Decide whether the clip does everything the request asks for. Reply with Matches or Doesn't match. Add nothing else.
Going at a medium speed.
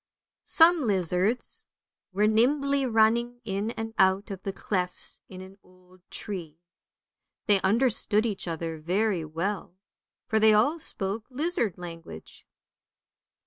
Doesn't match